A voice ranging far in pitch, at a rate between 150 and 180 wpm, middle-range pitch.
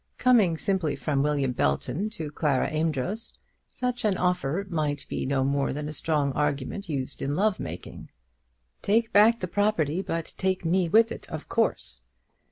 Yes: wide, 5.8 semitones; average, 165 wpm; medium, 165 Hz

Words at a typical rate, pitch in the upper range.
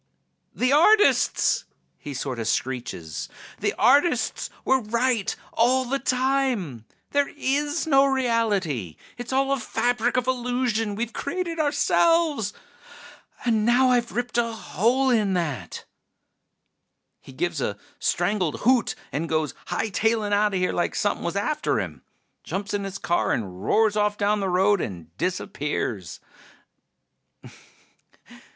No: slow, 125 wpm; high, 220 Hz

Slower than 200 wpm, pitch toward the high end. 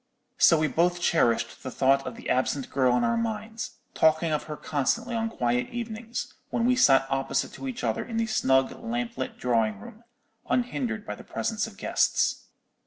Yes: average, 185 wpm; high, 200 Hz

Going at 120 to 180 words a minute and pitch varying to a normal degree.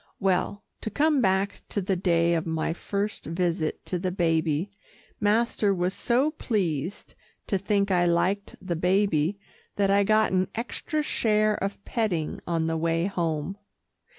Yes: average, 150 wpm; average, 3.3 semitones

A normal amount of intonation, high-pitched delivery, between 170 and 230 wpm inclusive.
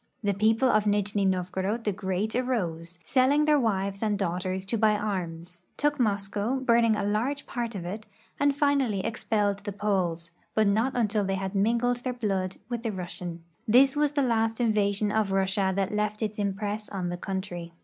Yes: average, 3.3 semitones; high, 210 Hz; average, 185 wpm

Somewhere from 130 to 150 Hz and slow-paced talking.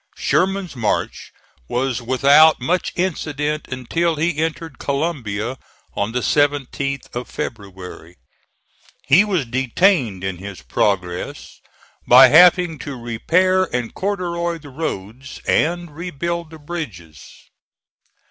Yes: medium, 140 Hz; slow, 110 wpm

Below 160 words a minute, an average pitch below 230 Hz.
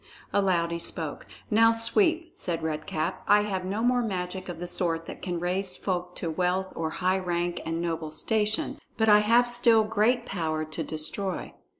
No: average, 185 wpm; medium, 185 Hz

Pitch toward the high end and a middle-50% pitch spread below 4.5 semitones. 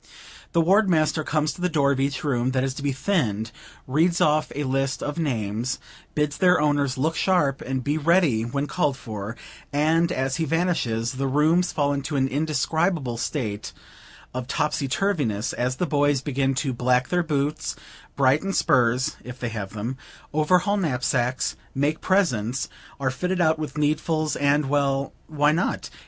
No: medium, 145 Hz; average, 3.5 semitones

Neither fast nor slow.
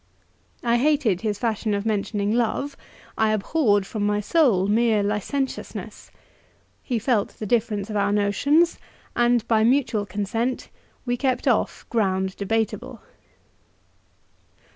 No: slow, 120 wpm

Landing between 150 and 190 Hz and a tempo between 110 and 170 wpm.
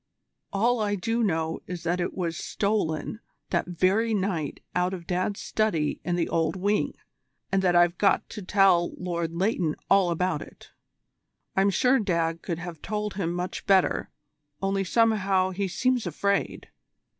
Yes: medium, 185 Hz; average, 155 wpm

